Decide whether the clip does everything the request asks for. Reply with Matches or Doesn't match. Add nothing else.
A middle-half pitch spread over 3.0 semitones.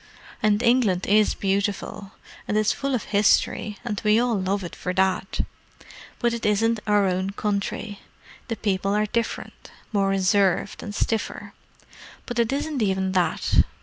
Doesn't match